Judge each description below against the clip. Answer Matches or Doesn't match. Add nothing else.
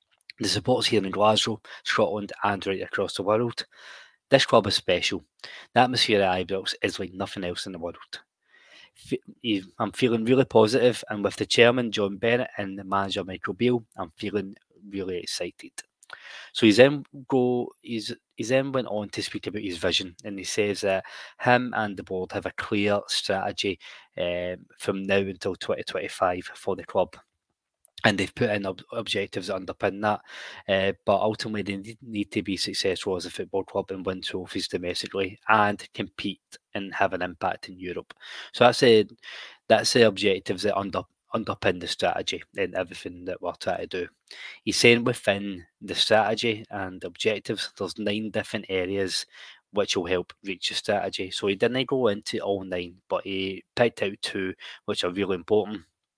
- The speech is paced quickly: Doesn't match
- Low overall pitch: Matches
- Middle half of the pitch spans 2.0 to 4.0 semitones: Matches